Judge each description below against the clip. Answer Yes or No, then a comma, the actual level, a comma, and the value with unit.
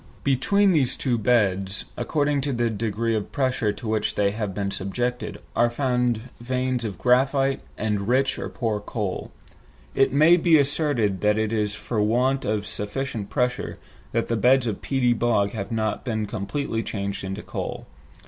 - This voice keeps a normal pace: Yes, average, 165 wpm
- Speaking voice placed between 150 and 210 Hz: No, low, 115 Hz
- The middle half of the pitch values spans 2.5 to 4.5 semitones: Yes, average, 4.0 semitones